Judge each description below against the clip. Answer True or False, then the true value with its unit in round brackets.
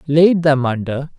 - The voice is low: False (145 Hz)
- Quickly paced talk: False (150 wpm)